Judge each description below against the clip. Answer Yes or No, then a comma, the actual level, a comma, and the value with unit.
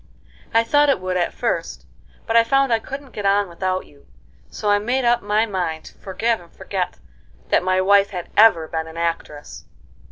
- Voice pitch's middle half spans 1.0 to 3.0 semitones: No, average, 4.3 semitones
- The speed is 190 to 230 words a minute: Yes, average, 195 wpm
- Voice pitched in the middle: No, high, 200 Hz